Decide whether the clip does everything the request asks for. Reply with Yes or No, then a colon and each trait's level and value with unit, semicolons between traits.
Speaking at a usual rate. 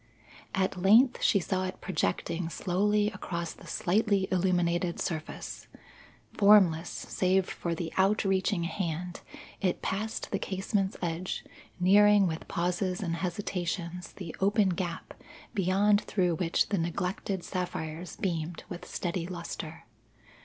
No: slow, 120 wpm